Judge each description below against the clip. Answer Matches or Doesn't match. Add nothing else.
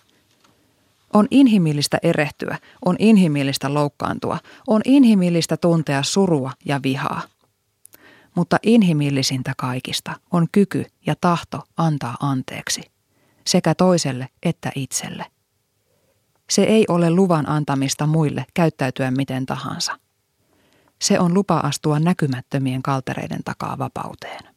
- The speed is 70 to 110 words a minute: Matches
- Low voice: Doesn't match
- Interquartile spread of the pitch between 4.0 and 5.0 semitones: Matches